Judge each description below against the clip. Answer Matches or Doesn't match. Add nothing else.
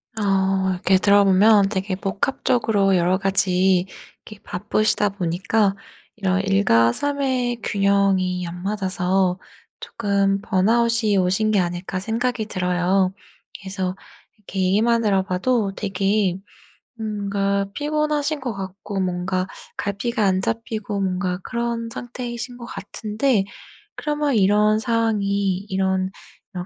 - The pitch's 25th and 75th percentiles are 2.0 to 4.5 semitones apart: Matches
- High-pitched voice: Matches